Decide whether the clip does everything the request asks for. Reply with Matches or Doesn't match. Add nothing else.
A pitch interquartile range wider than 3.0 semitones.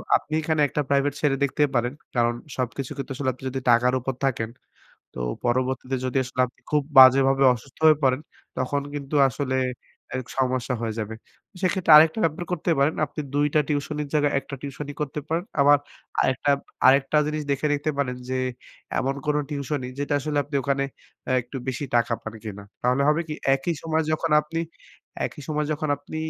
Doesn't match